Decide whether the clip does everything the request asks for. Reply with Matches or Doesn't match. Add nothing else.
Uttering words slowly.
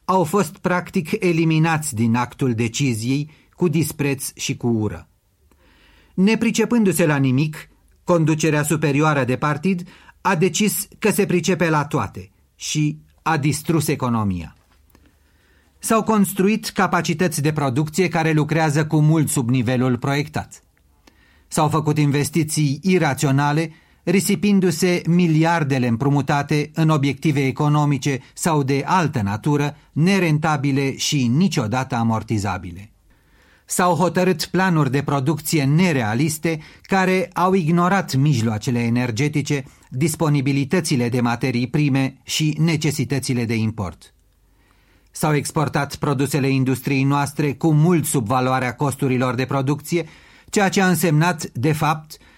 Matches